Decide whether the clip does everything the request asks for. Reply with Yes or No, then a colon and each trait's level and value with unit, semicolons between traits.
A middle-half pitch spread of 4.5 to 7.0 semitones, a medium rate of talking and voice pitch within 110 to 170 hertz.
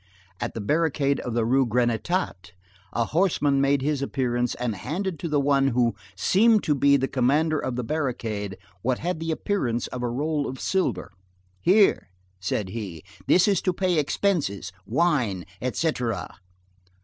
Yes: average, 5.2 semitones; average, 160 wpm; low, 135 Hz